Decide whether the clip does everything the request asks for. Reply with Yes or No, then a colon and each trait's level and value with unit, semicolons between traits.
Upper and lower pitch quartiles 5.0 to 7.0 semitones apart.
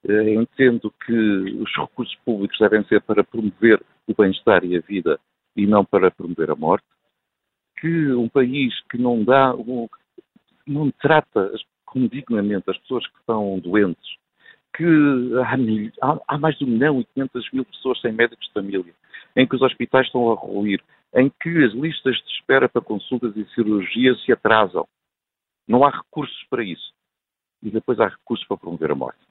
No: average, 3.9 semitones